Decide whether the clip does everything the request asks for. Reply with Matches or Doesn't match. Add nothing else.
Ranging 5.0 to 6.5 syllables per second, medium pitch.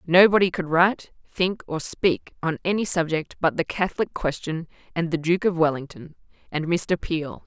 Doesn't match